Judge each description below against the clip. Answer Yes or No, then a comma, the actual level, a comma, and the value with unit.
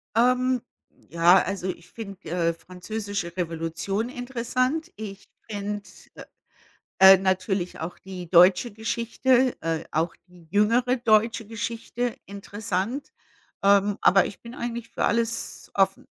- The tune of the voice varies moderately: Yes, average, 4.3 semitones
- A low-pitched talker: No, high, 205 Hz